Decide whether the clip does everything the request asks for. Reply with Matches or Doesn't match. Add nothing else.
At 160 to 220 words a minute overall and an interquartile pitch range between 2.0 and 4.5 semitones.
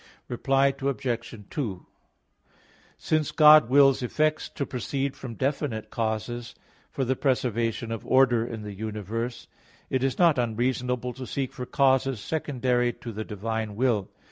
Doesn't match